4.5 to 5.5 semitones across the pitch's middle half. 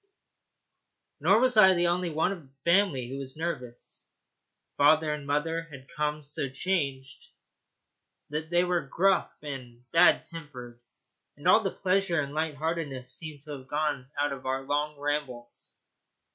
No: average, 3.7 semitones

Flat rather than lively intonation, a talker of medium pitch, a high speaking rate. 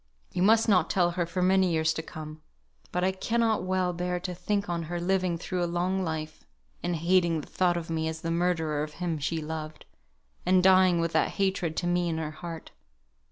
Yes: narrow, 2.3 semitones; medium, 175 Hz; fast, 210 wpm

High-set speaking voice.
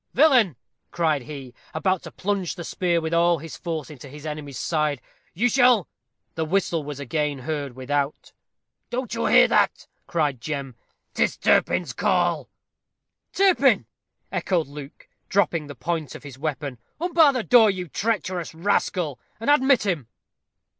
No: medium, 160 Hz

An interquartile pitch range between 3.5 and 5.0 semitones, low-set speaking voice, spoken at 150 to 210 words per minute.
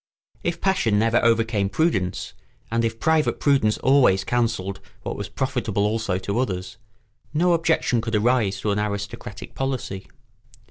No: average, 4.4 semitones; low, 115 Hz; average, 140 wpm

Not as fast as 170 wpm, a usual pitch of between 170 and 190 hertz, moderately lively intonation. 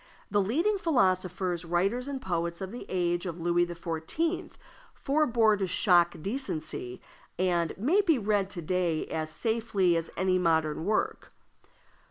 Yes: average, 140 wpm; medium, 185 Hz; average, 5.0 semitones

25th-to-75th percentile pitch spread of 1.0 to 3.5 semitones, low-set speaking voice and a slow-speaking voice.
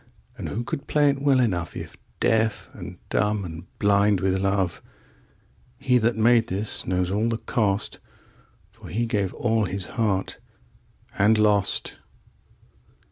Yes: average, 3.2 semitones; low, 105 Hz; slow, 130 wpm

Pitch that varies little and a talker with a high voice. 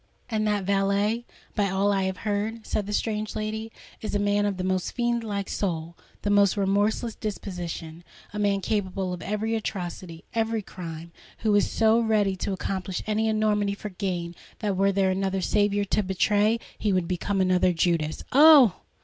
Yes: narrow, 2.3 semitones; high, 200 Hz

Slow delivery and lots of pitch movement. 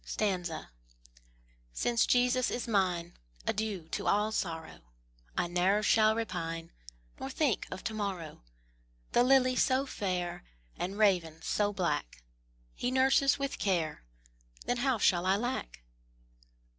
Yes: slow, 120 wpm; wide, 5.7 semitones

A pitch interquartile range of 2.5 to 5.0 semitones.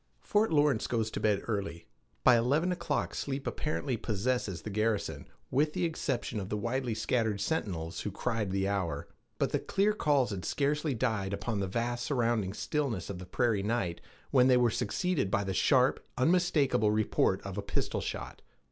No: wide, 5.4 semitones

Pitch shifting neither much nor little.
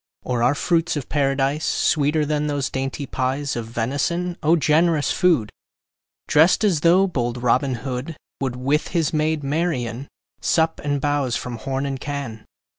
Yes: average, 3.5 semitones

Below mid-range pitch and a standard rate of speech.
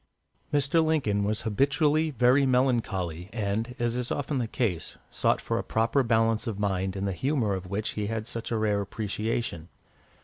Yes: low, 115 Hz; average, 175 wpm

